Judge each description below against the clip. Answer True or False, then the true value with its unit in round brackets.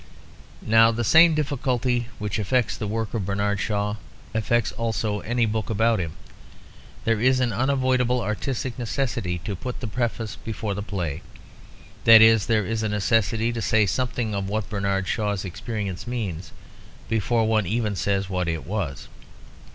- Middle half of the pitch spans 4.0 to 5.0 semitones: False (2.8 semitones)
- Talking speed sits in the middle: True (160 wpm)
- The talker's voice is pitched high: False (110 Hz)